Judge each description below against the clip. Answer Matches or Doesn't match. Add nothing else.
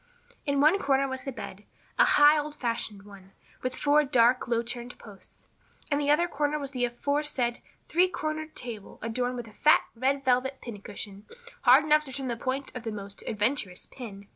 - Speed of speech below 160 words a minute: Doesn't match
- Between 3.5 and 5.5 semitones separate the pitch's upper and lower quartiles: Matches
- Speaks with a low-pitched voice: Doesn't match